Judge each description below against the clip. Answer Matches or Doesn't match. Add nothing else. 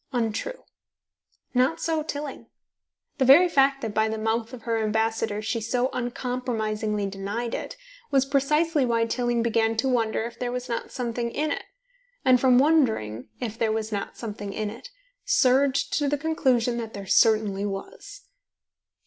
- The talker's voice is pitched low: Doesn't match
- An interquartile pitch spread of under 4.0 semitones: Matches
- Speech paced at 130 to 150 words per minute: Doesn't match